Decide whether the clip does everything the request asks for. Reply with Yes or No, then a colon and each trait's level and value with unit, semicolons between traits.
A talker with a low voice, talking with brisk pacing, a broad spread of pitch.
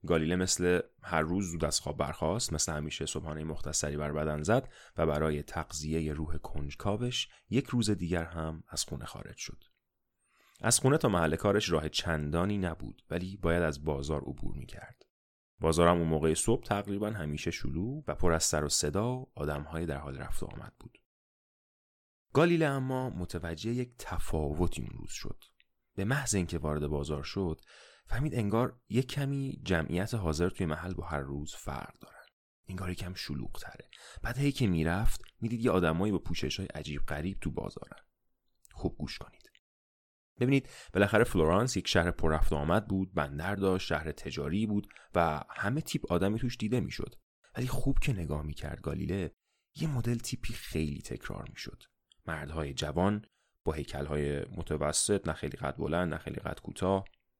Yes: very low, 90 Hz; fast, 165 wpm; wide, 6.0 semitones